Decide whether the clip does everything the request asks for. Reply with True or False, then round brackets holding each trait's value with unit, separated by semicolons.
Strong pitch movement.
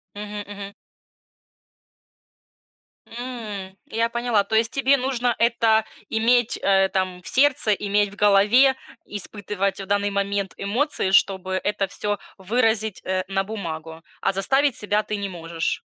False (2.9 semitones)